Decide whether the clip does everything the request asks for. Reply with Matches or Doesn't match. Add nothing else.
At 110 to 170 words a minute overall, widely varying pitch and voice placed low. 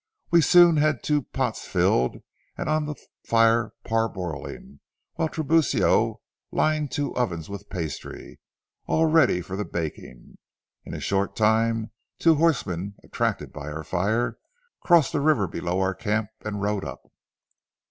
Matches